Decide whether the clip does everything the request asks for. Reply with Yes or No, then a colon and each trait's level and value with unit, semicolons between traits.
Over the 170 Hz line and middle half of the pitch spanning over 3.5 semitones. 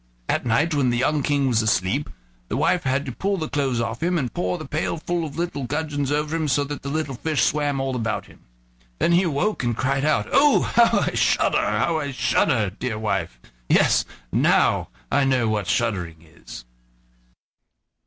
No: medium, 140 Hz; average, 4.8 semitones